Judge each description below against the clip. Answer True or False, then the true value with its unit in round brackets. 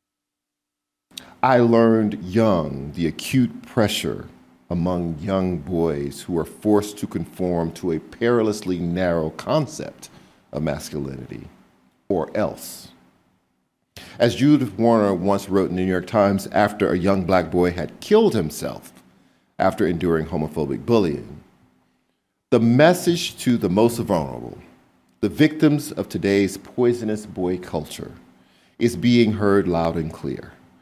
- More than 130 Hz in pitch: False (90 Hz)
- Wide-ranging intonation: True (6.0 semitones)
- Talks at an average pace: False (125 wpm)